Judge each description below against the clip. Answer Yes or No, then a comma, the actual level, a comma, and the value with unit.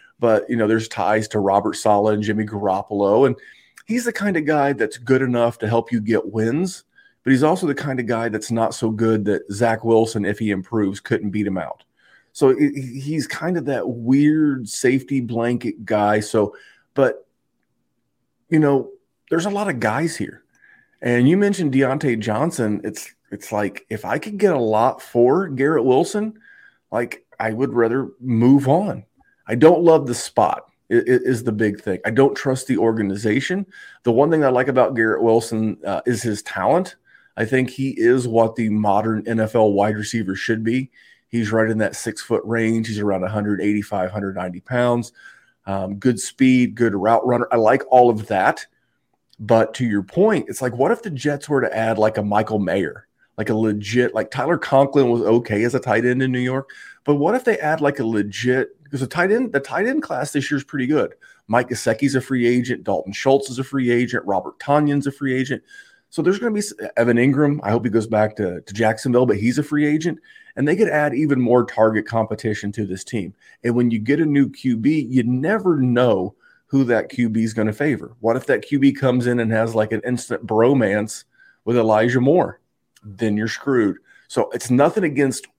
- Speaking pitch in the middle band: No, low, 120 Hz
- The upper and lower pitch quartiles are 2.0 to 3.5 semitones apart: No, average, 4.2 semitones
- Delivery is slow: No, average, 200 wpm